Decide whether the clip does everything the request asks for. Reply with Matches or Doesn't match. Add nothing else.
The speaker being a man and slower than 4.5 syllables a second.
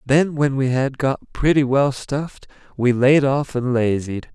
Matches